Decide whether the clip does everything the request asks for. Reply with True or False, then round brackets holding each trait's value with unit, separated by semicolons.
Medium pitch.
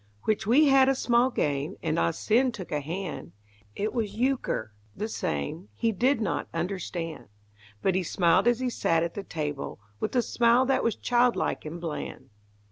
False (195 Hz)